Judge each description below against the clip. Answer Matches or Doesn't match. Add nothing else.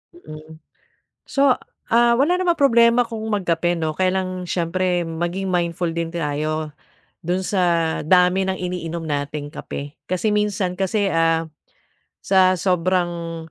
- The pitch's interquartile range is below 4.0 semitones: Matches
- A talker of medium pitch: Matches